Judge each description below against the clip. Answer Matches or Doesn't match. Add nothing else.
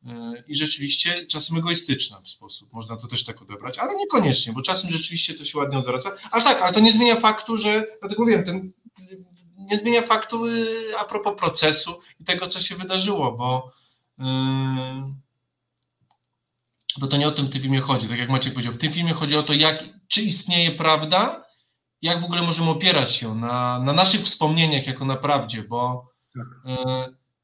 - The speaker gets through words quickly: Matches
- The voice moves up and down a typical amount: Doesn't match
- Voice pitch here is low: Doesn't match